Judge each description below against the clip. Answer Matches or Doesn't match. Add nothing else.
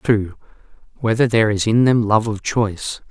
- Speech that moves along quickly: Doesn't match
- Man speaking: Matches